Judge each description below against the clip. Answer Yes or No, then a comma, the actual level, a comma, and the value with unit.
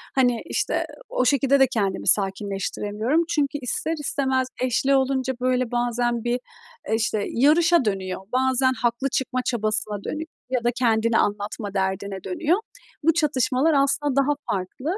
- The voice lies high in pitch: Yes, very high, 250 Hz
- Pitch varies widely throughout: No, average, 4.3 semitones